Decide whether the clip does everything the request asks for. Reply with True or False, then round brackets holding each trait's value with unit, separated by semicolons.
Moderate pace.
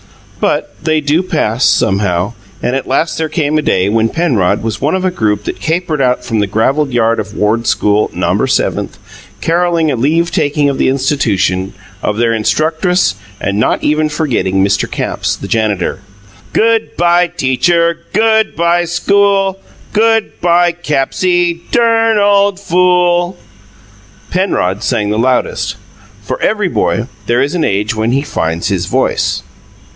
True (155 wpm)